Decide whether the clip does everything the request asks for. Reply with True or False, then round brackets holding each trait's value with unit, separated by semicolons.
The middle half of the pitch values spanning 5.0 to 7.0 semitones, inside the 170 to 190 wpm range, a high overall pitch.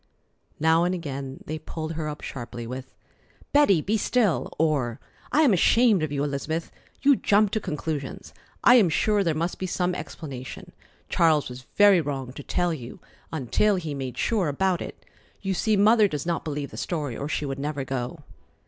False (5.5 semitones; 185 wpm; 160 Hz)